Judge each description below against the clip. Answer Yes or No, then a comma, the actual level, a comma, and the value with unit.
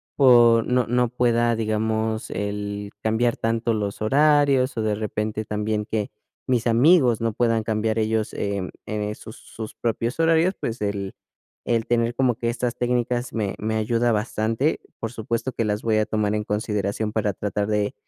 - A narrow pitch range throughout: Yes, narrow, 2.1 semitones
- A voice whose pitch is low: Yes, low, 110 Hz